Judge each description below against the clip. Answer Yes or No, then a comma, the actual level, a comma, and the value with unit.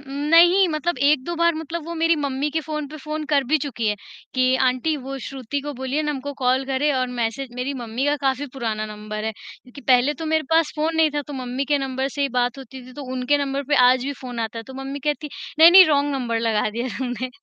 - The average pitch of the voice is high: Yes, very high, 275 Hz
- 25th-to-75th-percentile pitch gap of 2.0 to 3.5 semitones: Yes, average, 3.1 semitones